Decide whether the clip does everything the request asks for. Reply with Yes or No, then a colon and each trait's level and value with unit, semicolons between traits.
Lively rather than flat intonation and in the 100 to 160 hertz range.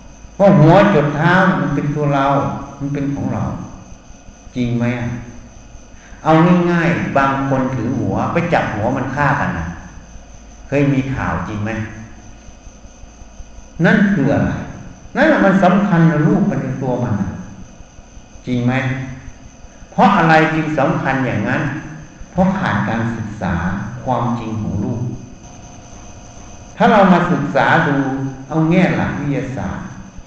Yes: wide, 6.4 semitones; low, 135 Hz